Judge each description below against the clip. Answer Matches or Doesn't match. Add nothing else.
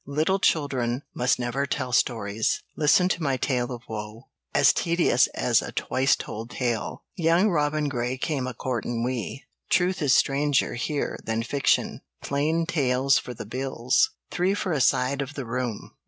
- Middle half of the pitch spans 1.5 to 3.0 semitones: Doesn't match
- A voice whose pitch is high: Doesn't match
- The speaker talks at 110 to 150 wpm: Doesn't match